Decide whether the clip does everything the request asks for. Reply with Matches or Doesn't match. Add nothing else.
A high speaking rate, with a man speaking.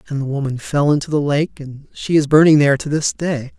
Matches